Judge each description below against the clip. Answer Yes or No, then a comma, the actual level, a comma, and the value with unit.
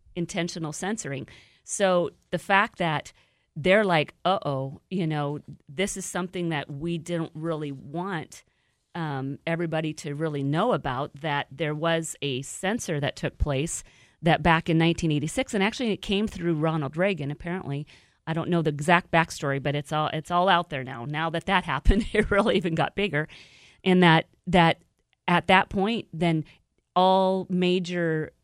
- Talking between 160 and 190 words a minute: Yes, average, 165 wpm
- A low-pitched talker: No, medium, 165 Hz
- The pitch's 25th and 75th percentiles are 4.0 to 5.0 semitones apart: No, average, 3.6 semitones